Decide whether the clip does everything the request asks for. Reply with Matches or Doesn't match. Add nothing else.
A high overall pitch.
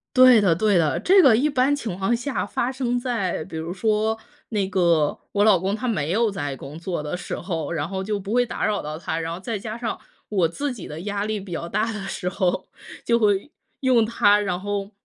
Matches